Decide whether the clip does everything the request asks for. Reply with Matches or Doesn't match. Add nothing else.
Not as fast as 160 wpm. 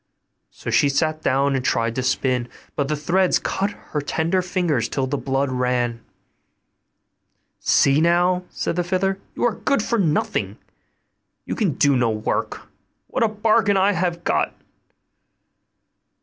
Matches